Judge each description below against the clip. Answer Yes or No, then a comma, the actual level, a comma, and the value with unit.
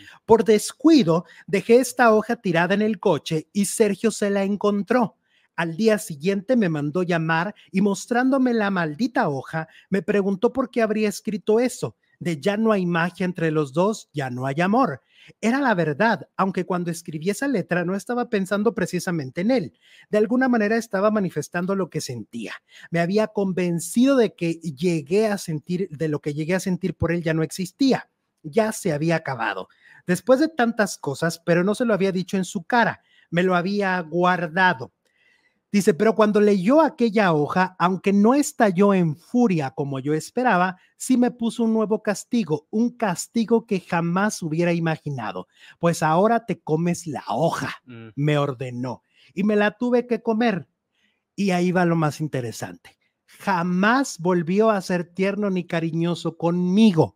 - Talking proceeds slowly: No, average, 170 wpm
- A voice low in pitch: No, high, 190 Hz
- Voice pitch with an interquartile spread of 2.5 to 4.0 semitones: No, average, 4.9 semitones